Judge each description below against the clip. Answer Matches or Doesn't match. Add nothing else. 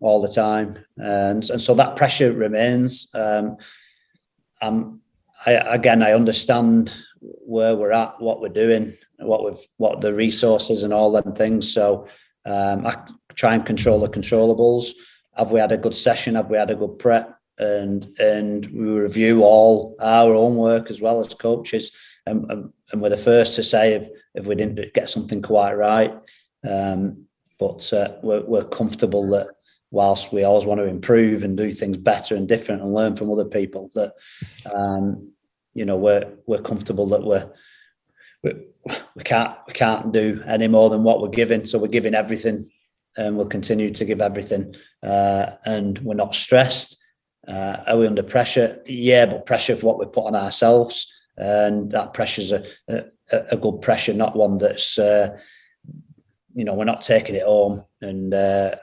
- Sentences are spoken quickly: Doesn't match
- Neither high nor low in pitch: Doesn't match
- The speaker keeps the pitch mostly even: Matches